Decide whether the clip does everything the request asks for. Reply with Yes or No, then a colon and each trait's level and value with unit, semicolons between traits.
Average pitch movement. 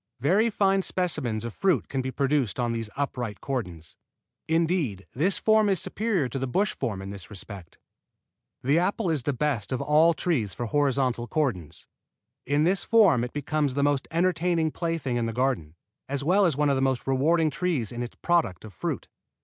No: wide, 5.9 semitones